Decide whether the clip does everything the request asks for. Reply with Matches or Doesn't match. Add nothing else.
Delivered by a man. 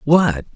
Matches